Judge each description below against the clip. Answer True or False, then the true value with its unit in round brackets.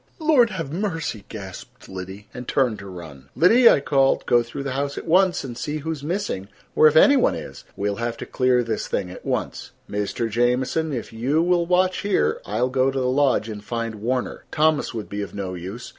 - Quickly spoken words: True (220 wpm)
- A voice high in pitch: False (125 Hz)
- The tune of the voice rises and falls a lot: True (7.0 semitones)